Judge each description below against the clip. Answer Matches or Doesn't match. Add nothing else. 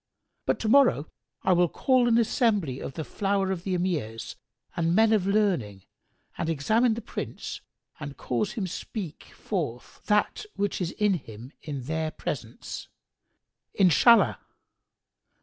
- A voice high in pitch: Doesn't match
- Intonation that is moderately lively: Doesn't match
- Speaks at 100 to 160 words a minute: Matches